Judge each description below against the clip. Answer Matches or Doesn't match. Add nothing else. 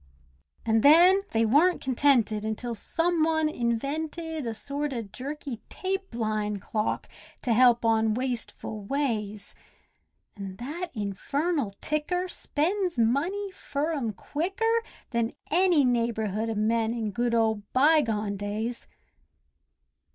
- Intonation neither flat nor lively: Doesn't match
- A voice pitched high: Matches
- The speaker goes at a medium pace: Doesn't match